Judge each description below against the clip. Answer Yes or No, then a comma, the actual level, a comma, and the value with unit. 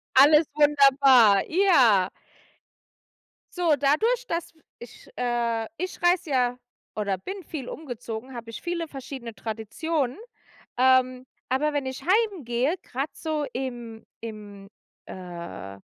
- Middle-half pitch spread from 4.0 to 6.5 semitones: Yes, average, 5.3 semitones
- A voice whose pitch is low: No, very high, 260 Hz